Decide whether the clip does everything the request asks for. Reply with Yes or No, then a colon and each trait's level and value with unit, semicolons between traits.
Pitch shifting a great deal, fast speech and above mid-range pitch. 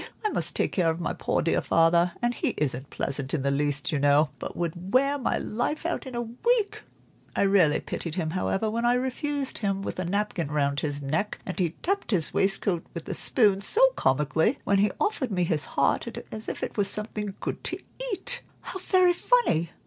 Yes: wide, 7.6 semitones; fast, 210 wpm; high, 195 Hz